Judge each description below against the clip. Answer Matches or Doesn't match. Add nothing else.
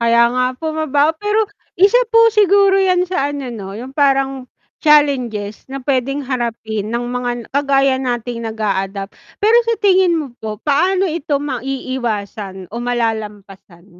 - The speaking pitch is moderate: Doesn't match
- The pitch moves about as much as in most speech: Doesn't match